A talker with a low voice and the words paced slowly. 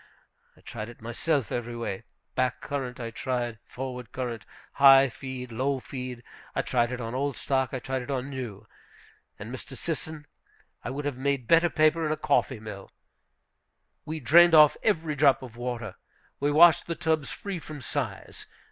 No: low, 130 Hz; average, 175 wpm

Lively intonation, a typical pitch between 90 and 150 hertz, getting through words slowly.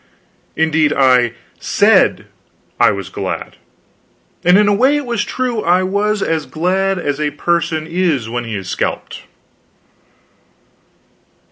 No: wide, 5.8 semitones; medium, 170 Hz; slow, 130 wpm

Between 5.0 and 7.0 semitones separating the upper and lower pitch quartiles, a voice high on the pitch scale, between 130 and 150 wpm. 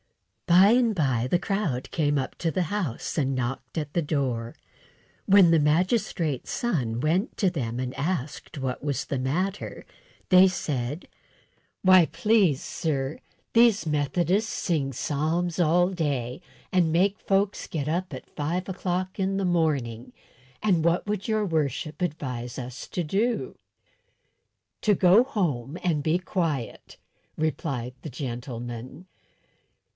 No: wide, 5.4 semitones; medium, 160 Hz; slow, 135 wpm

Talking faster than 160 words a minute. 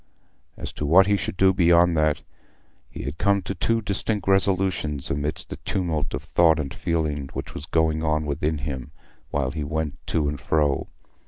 Yes: average, 180 wpm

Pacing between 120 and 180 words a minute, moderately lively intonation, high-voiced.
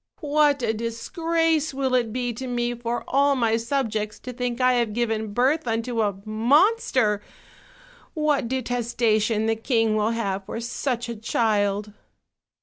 Yes: average, 145 wpm; average, 3.0 semitones; high, 235 Hz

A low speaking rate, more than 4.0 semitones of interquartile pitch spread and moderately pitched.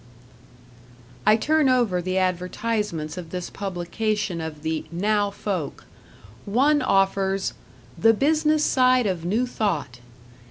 No: slow, 115 wpm; average, 4.6 semitones; high, 200 Hz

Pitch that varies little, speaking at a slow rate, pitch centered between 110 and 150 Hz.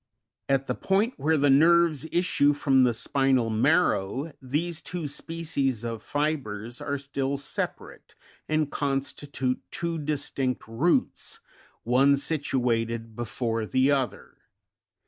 No: average, 3.5 semitones; slow, 125 wpm; medium, 140 Hz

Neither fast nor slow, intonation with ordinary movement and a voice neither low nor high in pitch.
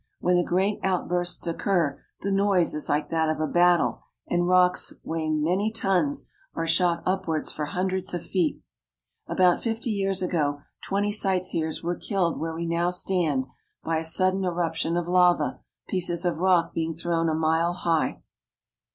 No: average, 170 wpm; narrow, 2.2 semitones; medium, 175 Hz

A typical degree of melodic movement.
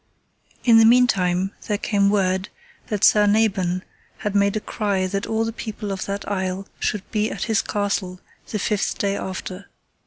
No: narrow, 2.0 semitones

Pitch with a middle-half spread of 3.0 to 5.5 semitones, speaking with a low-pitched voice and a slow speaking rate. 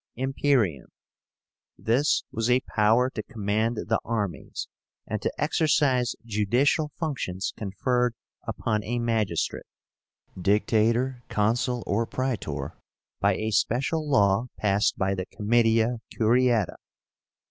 Yes: average, 3.3 semitones; low, 115 Hz; slow, 105 wpm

